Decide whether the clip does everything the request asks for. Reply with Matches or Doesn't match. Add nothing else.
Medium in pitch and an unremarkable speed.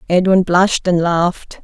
Matches